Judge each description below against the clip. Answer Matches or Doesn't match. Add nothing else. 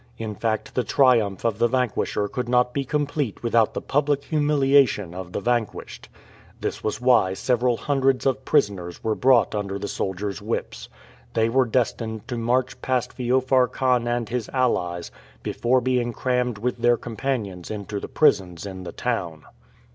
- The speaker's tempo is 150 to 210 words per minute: Matches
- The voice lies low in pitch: Matches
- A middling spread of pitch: Matches